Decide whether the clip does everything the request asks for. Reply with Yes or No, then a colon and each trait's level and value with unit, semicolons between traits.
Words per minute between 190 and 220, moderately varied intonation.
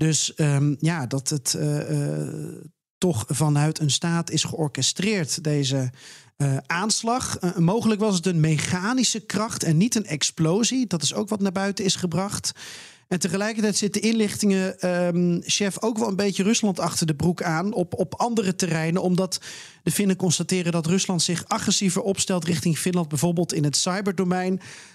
No: average, 165 wpm; average, 4.2 semitones